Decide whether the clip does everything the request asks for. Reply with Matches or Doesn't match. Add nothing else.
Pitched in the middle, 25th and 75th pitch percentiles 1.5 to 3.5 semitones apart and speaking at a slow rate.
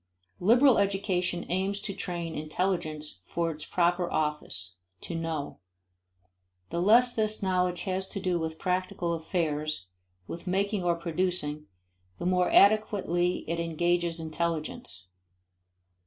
Matches